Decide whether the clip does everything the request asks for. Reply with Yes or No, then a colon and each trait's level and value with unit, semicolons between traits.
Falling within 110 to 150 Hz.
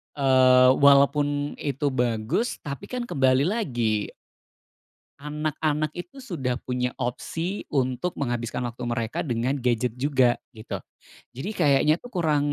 Yes: low, 135 Hz